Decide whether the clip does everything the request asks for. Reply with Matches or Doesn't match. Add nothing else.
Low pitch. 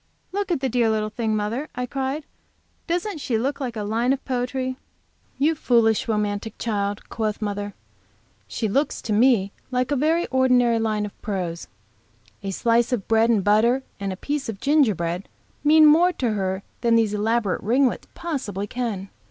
Doesn't match